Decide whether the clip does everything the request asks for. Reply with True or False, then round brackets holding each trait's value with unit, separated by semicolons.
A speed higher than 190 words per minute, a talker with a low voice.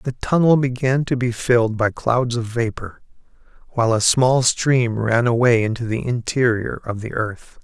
False (175 wpm; 120 Hz)